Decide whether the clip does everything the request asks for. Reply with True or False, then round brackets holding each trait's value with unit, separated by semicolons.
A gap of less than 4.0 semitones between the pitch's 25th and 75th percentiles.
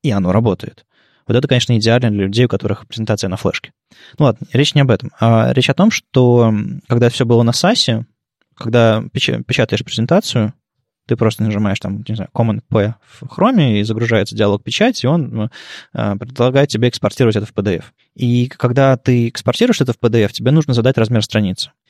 True (3.2 semitones)